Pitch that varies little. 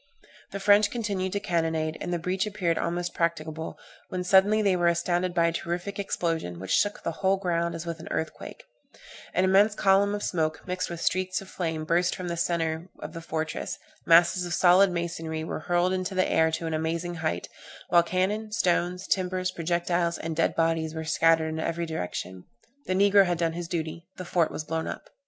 Yes: narrow, 2.2 semitones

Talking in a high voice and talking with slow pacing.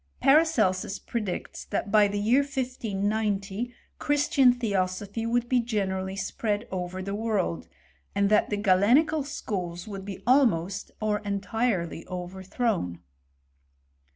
Yes: high, 205 Hz; slow, 115 wpm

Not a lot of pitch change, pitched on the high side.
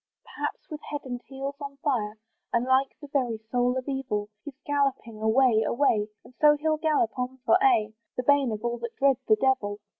No: average, 3.6 semitones; very high, 260 Hz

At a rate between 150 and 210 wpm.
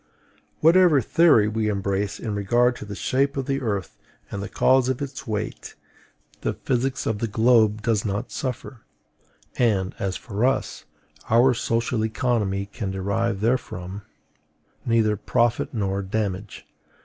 No: average, 140 wpm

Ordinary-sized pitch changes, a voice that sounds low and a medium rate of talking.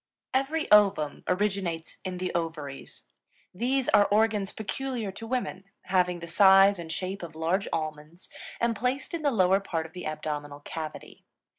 No: average, 4.8 semitones; high, 190 Hz; average, 155 wpm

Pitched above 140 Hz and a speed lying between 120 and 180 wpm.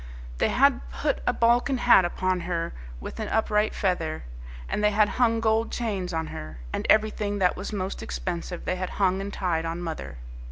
No: high, 190 Hz; average, 190 wpm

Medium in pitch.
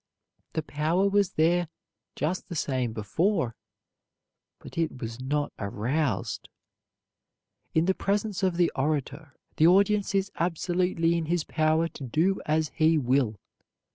Yes: medium, 160 Hz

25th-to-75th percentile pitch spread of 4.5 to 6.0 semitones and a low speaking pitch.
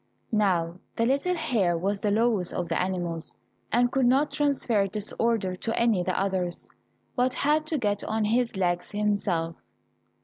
No: average, 5.0 semitones; high, 210 Hz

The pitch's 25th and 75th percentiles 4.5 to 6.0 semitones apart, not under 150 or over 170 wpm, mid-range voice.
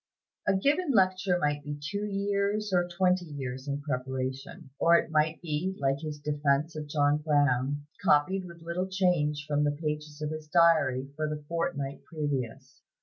No: average, 3.6 semitones; average, 165 wpm; medium, 150 Hz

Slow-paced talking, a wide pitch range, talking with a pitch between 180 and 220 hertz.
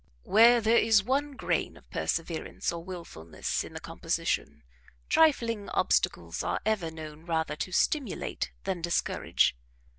Yes: slow, 130 wpm; wide, 6.1 semitones; medium, 185 Hz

